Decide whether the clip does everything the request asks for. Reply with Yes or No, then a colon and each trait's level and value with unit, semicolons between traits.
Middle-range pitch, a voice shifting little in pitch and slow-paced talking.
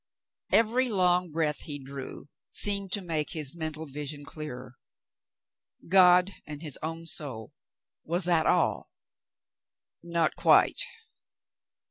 No: medium, 160 Hz; average, 3.5 semitones; slow, 115 wpm